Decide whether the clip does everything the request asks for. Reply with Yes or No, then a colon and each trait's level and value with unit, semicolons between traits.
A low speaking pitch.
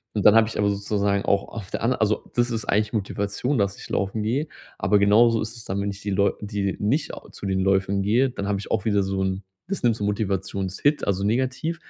Yes: low, 105 Hz